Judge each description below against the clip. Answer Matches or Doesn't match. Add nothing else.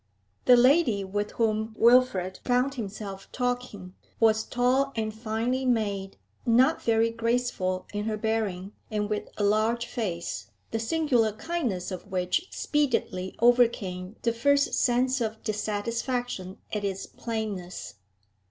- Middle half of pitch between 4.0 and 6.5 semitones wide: Doesn't match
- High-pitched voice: Matches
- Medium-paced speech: Doesn't match